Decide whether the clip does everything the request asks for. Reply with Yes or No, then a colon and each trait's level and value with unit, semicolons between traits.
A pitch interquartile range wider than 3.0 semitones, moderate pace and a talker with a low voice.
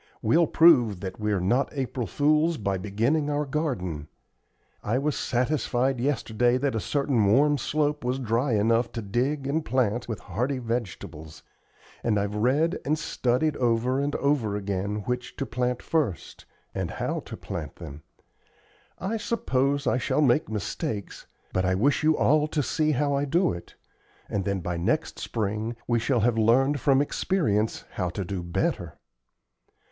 Yes: wide, 5.5 semitones; average, 160 wpm; low, 125 Hz